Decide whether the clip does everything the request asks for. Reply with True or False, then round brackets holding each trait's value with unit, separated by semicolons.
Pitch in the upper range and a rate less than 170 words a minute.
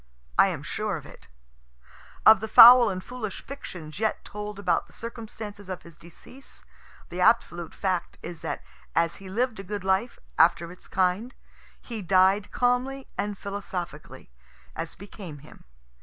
True (200 Hz; 155 wpm)